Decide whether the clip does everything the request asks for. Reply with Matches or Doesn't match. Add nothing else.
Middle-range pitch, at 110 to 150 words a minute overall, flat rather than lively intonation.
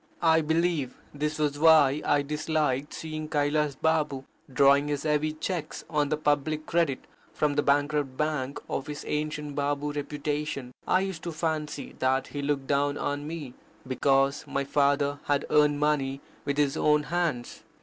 Doesn't match